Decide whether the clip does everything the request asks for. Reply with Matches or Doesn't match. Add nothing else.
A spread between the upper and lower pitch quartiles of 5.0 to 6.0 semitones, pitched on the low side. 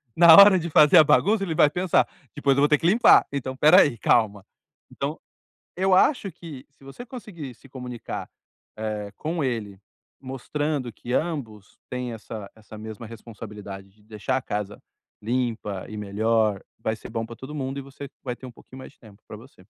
Matches